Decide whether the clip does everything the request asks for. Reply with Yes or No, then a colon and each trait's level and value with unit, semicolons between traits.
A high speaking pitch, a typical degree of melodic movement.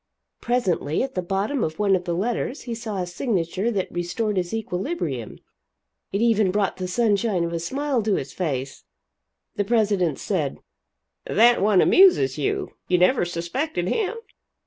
Yes: high, 195 Hz; average, 5.0 semitones